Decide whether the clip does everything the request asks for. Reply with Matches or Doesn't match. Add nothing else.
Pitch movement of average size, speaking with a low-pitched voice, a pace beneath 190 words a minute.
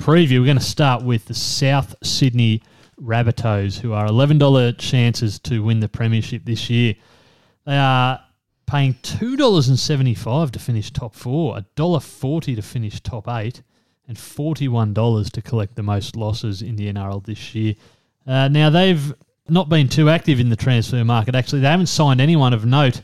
Matches